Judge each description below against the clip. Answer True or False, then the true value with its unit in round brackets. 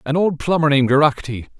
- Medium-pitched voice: True (145 Hz)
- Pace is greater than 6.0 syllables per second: True (6.4 syllables/s)